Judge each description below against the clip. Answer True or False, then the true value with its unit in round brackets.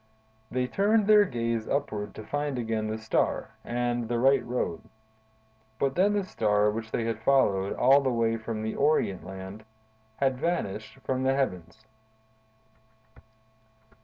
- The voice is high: False (120 Hz)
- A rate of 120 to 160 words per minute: True (140 wpm)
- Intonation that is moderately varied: True (4.1 semitones)